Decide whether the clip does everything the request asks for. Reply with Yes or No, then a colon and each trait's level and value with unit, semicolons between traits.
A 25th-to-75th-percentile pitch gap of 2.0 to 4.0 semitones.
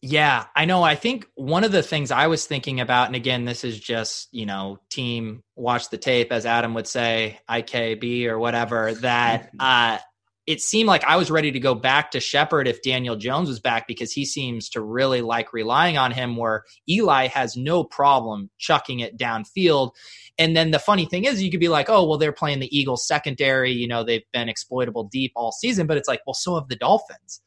No: average, 4.5 semitones